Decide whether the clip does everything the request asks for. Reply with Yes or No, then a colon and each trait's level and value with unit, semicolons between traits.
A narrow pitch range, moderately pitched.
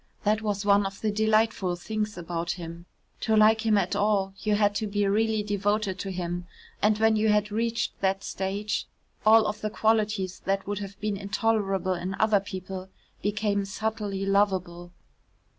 No: narrow, 1.9 semitones; high, 205 Hz